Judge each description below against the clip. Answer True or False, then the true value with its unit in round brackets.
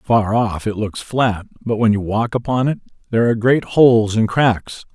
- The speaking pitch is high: False (110 Hz)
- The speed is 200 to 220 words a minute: True (205 wpm)